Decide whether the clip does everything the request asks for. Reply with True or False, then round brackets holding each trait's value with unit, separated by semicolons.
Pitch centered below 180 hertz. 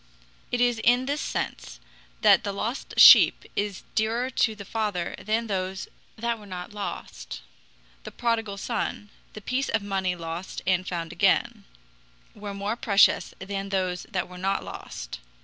False (200 Hz)